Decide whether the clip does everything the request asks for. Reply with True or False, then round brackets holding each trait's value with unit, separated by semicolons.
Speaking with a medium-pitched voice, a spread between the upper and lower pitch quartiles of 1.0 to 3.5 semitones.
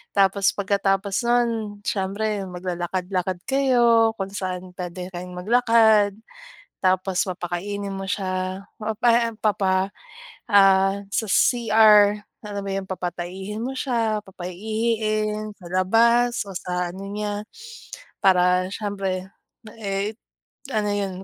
False (200 Hz; 2.6 semitones)